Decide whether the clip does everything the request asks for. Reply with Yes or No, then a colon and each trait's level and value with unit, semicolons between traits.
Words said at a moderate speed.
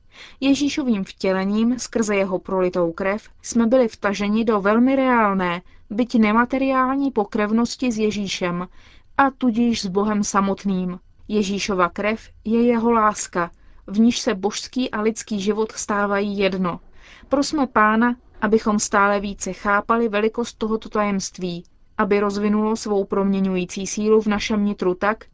Yes: average, 130 wpm